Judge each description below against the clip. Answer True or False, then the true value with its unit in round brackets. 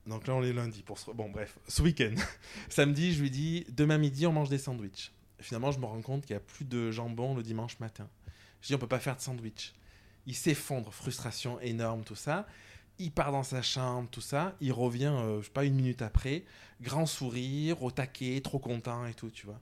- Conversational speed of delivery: False (230 wpm)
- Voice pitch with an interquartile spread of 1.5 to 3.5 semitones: False (4.1 semitones)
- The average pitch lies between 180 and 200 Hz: False (125 Hz)